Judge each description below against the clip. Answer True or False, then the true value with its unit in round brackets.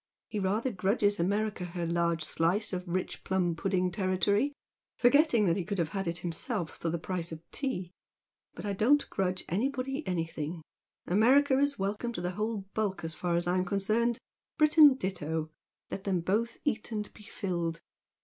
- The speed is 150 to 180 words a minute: True (170 wpm)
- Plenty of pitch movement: False (4.2 semitones)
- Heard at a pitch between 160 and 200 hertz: True (190 Hz)